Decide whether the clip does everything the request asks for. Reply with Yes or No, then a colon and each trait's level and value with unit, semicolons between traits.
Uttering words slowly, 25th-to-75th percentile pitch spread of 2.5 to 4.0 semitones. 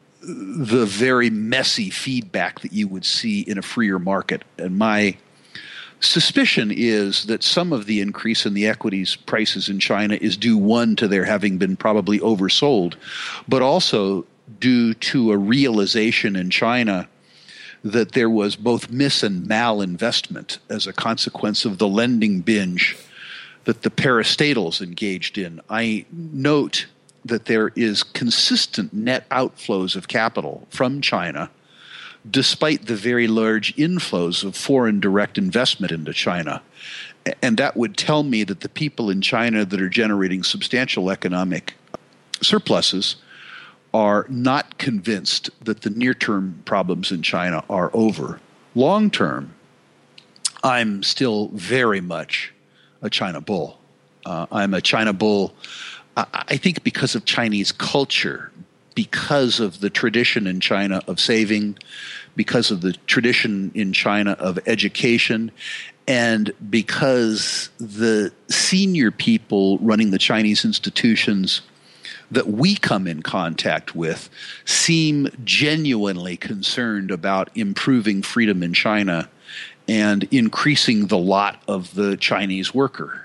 No: slow, 130 wpm; average, 5.1 semitones